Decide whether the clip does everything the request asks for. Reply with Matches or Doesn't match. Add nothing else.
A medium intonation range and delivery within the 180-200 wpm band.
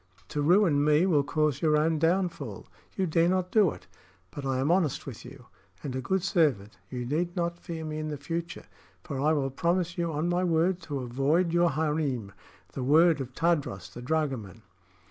Matches